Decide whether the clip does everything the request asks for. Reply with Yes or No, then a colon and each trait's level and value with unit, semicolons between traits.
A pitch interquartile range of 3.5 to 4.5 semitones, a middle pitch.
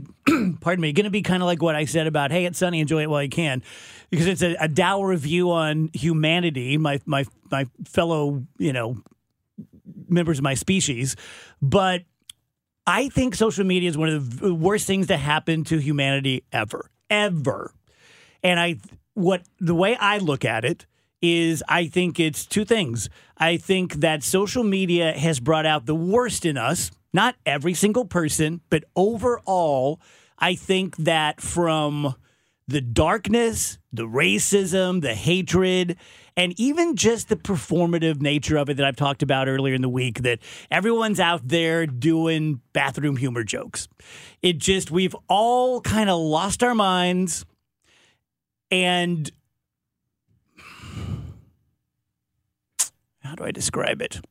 Yes: average, 4.0 semitones; medium, 165 Hz